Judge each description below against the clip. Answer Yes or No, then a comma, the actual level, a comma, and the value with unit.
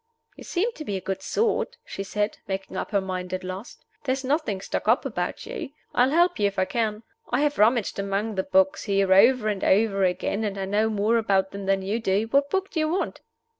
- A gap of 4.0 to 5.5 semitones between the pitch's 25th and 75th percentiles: Yes, average, 4.5 semitones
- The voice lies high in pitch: Yes, high, 205 Hz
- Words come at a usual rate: No, fast, 230 wpm